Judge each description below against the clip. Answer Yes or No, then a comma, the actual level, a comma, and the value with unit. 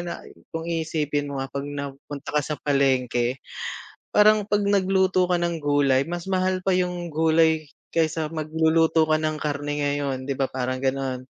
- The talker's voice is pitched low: No, medium, 155 Hz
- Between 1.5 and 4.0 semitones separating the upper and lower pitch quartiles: Yes, average, 3.5 semitones